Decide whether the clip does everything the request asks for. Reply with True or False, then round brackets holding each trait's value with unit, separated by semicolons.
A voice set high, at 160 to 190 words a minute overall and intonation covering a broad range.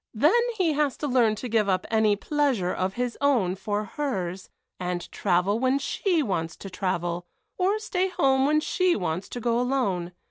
True (225 Hz; 180 wpm; 7.3 semitones)